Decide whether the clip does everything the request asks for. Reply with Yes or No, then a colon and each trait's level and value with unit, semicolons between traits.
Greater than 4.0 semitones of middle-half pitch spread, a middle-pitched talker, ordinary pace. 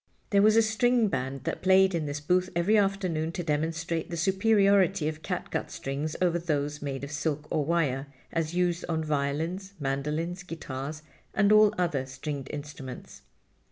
Yes: average, 4.4 semitones; medium, 165 Hz; average, 165 wpm